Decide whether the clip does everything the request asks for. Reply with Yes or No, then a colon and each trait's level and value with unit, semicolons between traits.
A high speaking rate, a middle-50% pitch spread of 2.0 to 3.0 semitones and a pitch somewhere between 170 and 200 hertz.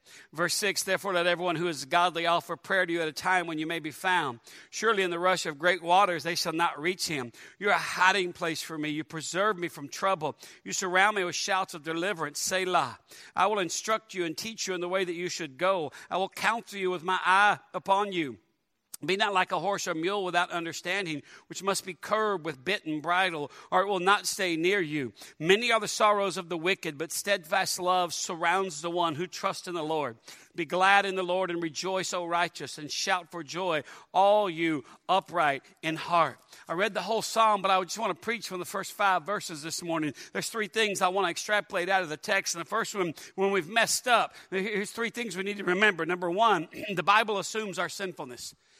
Yes: fast, 230 wpm; average, 2.7 semitones; medium, 185 Hz